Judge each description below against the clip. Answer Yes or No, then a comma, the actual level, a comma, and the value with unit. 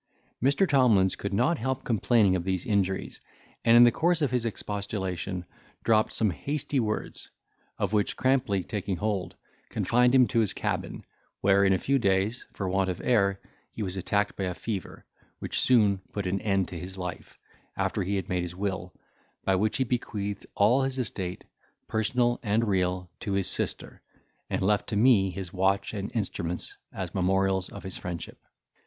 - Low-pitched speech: Yes, low, 100 Hz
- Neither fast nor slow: Yes, average, 175 wpm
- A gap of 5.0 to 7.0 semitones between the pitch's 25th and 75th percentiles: No, average, 3.6 semitones